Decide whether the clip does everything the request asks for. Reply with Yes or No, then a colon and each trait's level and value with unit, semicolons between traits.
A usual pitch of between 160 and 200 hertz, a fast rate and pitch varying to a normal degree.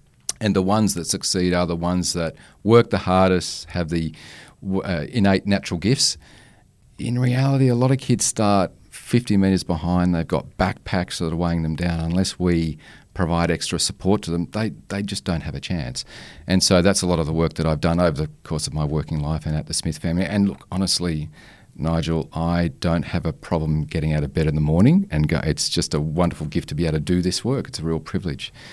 No: very low, 85 Hz; fast, 225 wpm; average, 3.1 semitones